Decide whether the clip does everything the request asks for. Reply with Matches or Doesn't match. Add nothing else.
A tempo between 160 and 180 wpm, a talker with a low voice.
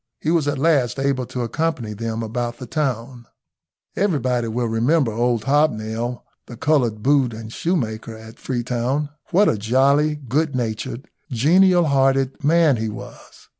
Doesn't match